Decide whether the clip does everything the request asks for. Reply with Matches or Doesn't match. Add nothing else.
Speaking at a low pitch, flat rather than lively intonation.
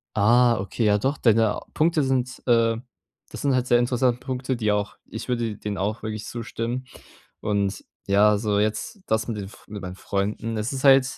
Doesn't match